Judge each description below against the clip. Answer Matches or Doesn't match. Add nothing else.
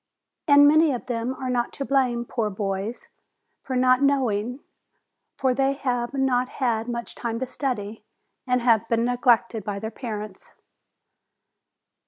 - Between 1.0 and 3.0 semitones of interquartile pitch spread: Matches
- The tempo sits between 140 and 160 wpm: Matches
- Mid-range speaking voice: Doesn't match